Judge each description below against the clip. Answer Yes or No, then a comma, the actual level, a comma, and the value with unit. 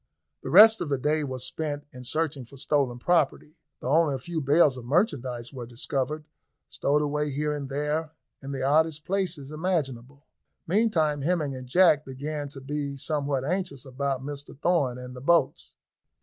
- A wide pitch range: No, average, 2.8 semitones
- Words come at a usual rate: Yes, average, 170 wpm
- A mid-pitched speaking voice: Yes, medium, 145 Hz